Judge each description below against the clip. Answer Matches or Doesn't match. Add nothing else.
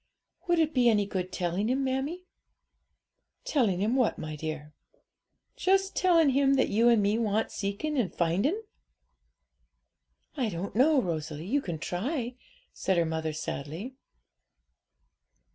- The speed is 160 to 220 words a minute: Doesn't match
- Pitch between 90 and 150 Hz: Doesn't match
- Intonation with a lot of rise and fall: Matches